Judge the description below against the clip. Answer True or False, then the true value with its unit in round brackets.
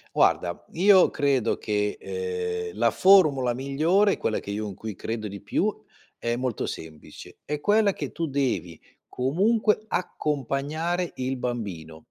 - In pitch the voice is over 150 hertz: False (135 Hz)